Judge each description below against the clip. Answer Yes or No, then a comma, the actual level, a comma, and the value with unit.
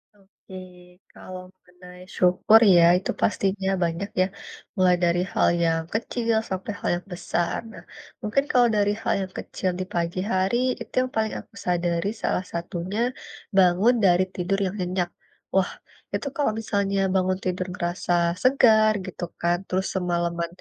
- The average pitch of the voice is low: No, medium, 185 Hz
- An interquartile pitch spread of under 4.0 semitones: Yes, average, 2.7 semitones